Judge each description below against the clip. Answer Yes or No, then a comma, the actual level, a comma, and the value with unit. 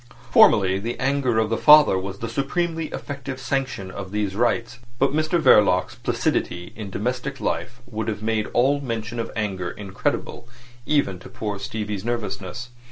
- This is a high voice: No, low, 115 Hz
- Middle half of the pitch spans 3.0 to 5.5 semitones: Yes, average, 4.7 semitones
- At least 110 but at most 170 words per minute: Yes, average, 160 wpm